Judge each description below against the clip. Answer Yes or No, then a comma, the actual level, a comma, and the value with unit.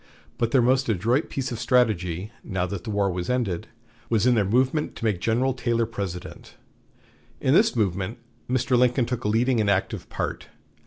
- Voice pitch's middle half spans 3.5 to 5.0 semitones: Yes, average, 4.1 semitones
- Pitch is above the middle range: No, low, 115 Hz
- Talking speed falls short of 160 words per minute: No, average, 180 wpm